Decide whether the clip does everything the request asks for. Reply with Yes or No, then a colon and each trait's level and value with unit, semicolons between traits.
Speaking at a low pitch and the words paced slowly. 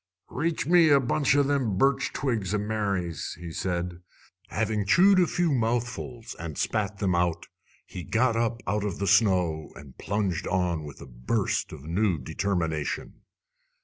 No: low, 100 Hz; average, 160 wpm